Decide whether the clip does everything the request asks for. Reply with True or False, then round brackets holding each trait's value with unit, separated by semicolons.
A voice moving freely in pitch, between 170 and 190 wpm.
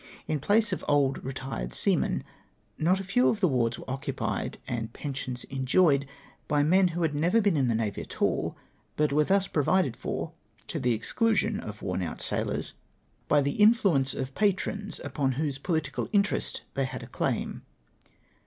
True (6.3 semitones; 175 wpm)